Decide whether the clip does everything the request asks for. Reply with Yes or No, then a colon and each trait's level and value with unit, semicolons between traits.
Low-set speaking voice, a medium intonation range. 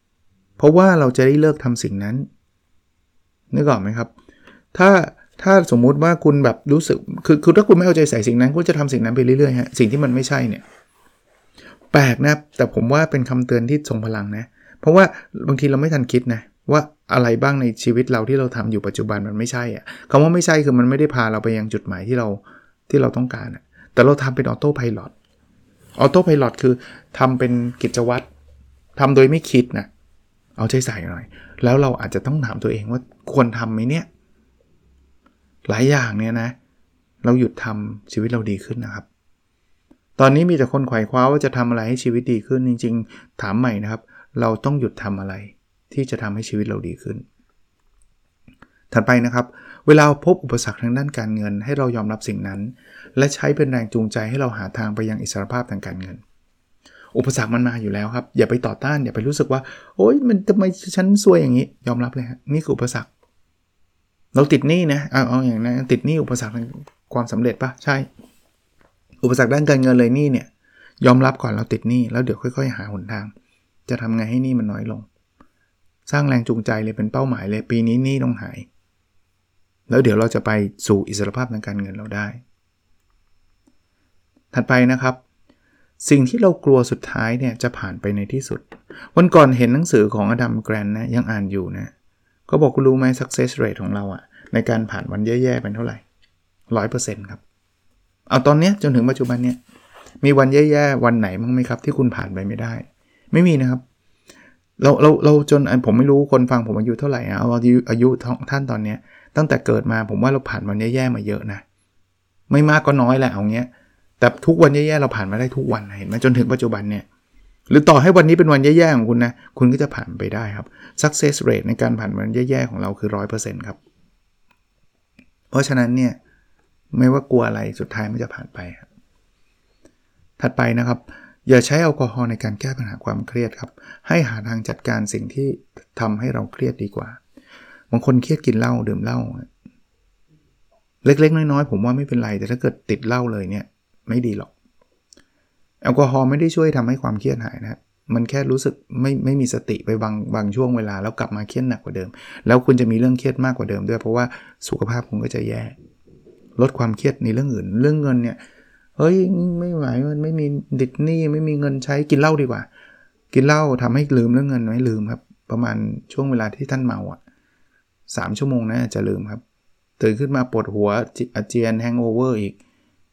Yes: low, 120 Hz; average, 3.9 semitones